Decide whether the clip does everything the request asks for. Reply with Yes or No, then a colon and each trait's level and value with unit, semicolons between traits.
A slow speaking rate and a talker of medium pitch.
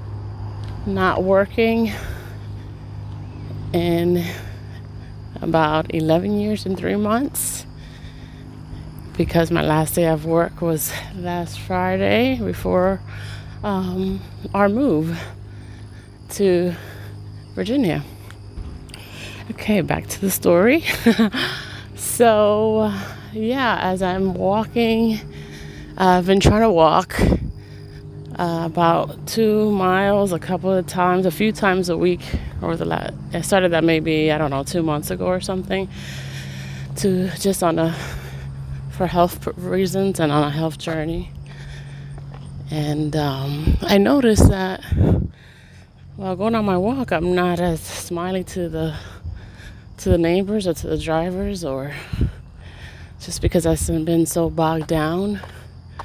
Yes: slow, 120 wpm; medium, 165 Hz